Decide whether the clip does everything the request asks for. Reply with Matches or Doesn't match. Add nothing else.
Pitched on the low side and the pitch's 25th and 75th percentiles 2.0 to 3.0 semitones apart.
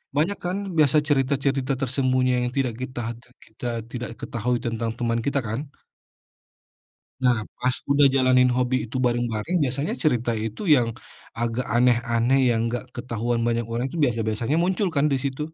Matches